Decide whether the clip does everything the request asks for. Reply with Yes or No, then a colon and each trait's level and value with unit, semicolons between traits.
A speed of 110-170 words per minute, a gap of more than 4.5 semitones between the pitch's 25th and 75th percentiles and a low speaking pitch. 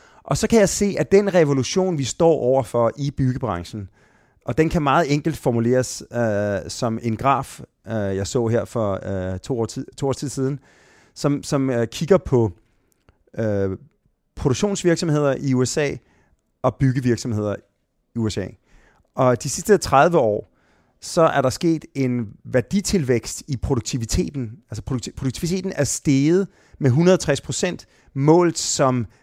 Yes: slow, 145 wpm; wide, 5.4 semitones; low, 130 Hz